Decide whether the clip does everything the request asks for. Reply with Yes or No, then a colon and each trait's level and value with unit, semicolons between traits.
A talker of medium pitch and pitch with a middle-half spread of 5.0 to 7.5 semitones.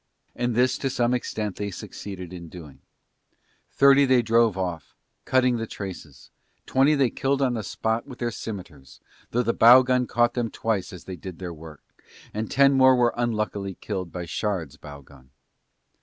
No: low, 110 Hz; wide, 5.4 semitones